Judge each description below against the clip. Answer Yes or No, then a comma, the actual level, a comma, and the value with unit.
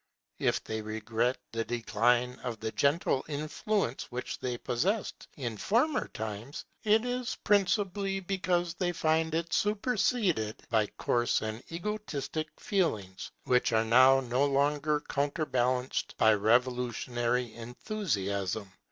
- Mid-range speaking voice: No, low, 130 Hz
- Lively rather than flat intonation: Yes, wide, 7.4 semitones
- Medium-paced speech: No, slow, 115 wpm